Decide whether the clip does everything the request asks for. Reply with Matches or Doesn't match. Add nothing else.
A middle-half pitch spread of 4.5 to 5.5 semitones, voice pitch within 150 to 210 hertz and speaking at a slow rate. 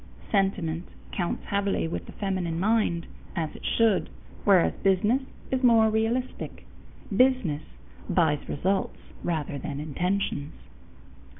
Matches